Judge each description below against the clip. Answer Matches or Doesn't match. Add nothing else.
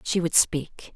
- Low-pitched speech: Doesn't match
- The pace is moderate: Matches